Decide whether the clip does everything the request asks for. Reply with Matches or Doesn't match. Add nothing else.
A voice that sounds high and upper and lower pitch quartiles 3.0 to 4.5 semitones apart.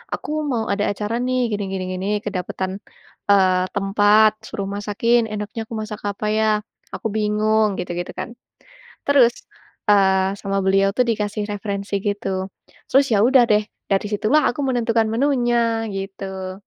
Doesn't match